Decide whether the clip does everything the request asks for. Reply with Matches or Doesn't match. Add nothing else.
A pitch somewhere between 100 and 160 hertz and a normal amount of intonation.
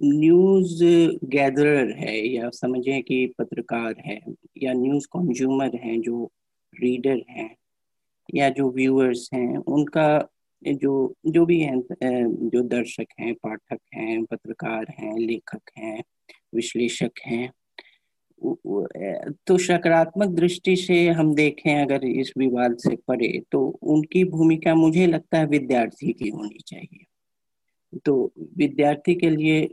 Matches